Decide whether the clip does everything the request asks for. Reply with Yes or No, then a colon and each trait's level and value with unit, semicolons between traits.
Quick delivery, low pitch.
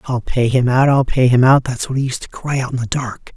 Yes: fast, 320 wpm; low, 125 Hz